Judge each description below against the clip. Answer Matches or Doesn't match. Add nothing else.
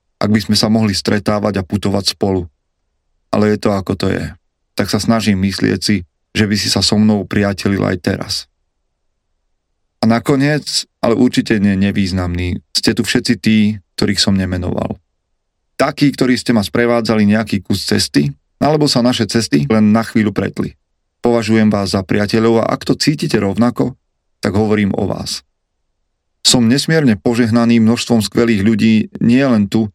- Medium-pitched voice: Doesn't match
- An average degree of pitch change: Matches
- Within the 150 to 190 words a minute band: Matches